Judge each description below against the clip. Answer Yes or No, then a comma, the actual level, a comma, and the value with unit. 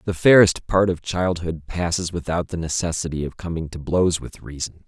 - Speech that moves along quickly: No, average, 185 wpm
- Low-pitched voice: Yes, very low, 85 Hz